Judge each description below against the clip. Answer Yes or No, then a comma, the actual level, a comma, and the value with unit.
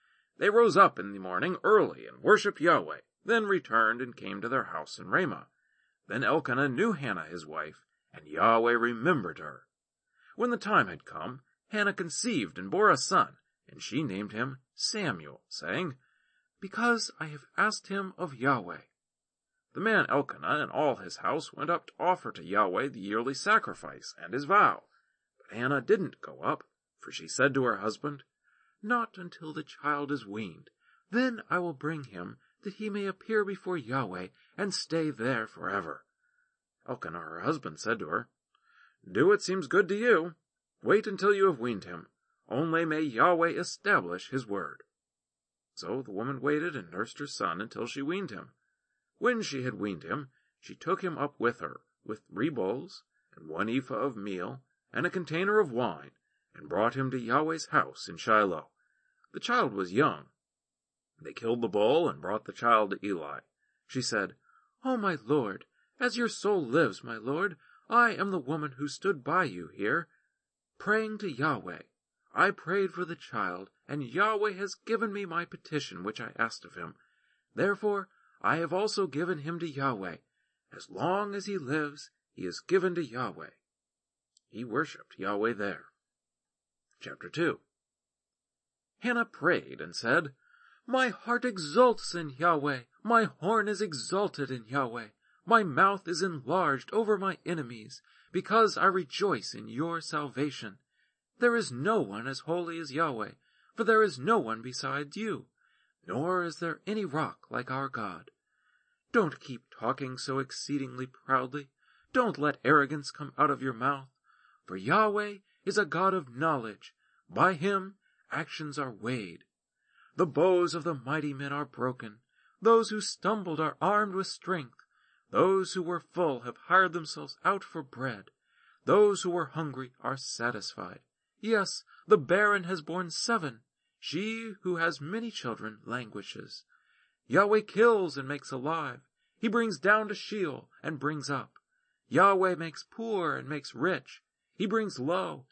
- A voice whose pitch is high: No, medium, 170 Hz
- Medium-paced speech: Yes, average, 160 wpm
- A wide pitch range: Yes, wide, 7.3 semitones